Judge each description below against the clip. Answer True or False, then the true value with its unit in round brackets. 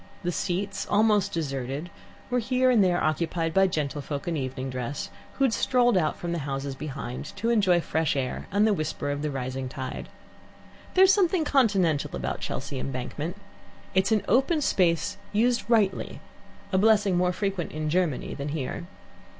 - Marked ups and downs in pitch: True (6.5 semitones)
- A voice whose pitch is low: False (175 Hz)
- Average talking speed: True (170 wpm)